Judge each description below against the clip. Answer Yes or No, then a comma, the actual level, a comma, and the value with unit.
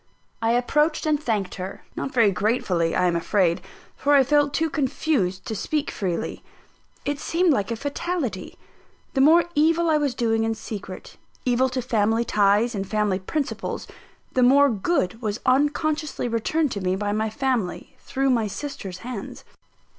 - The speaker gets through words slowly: No, average, 160 wpm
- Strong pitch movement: Yes, wide, 6.0 semitones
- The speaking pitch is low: No, high, 240 Hz